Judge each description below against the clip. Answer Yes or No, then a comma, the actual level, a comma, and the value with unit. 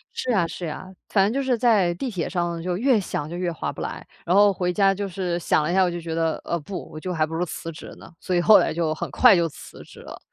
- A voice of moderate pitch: Yes, medium, 175 Hz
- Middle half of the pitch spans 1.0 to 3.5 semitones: Yes, average, 2.9 semitones